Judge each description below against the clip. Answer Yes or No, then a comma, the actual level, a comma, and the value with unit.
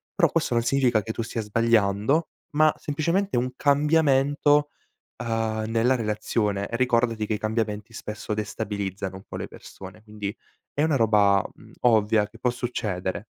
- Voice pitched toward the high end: No, low, 115 Hz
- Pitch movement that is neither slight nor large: Yes, average, 3.4 semitones